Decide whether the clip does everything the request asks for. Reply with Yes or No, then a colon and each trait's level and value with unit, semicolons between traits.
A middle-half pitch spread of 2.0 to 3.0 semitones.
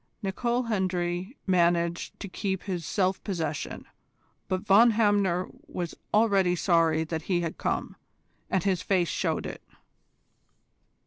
Yes: average, 2.7 semitones